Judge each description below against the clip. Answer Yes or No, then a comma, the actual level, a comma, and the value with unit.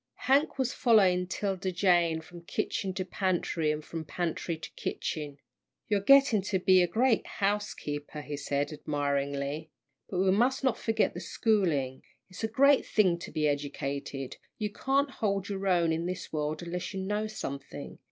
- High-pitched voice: No, medium, 180 Hz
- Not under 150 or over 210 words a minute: Yes, average, 165 wpm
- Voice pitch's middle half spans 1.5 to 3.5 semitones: No, wide, 5.4 semitones